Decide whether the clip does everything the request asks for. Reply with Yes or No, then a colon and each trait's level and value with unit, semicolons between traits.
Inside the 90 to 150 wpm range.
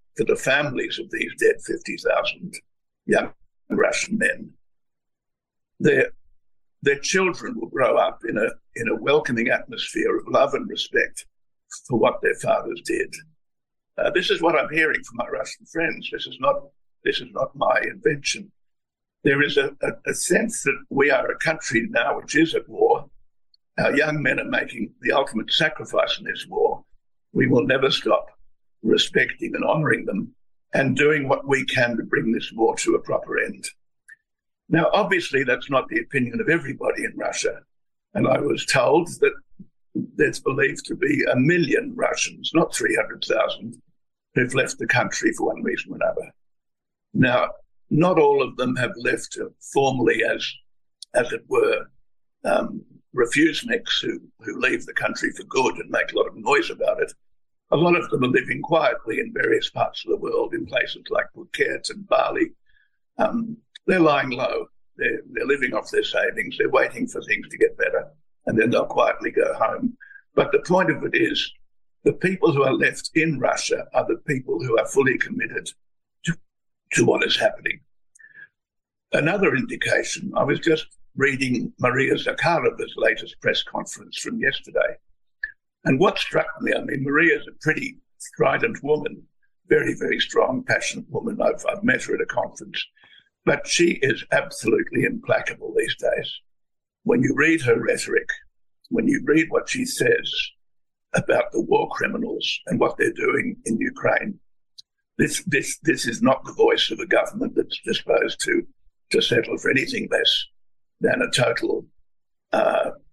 No: average, 165 wpm